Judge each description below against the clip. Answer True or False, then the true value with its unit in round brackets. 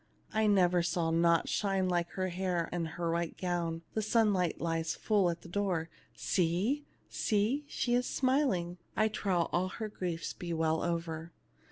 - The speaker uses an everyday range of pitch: True (3.6 semitones)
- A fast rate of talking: False (165 wpm)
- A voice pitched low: False (180 Hz)